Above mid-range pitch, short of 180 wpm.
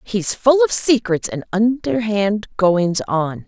Yes: high, 200 Hz; average, 140 wpm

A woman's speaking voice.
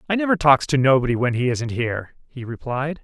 No: male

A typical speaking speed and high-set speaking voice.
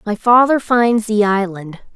Yes: average, 155 wpm; high, 215 Hz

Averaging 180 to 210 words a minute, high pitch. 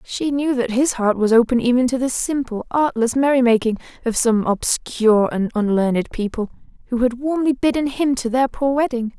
Yes: average, 185 wpm; high, 245 Hz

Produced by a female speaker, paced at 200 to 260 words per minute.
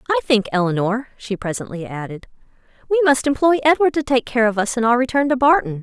Yes: female; fast, 205 wpm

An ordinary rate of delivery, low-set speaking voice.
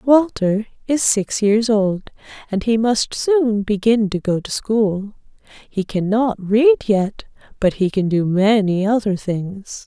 No: average, 150 wpm; high, 210 Hz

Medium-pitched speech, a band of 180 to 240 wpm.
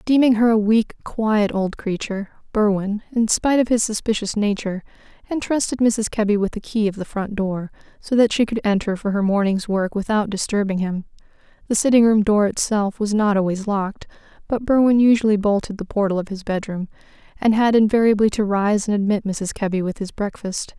No: high, 210 Hz; average, 190 wpm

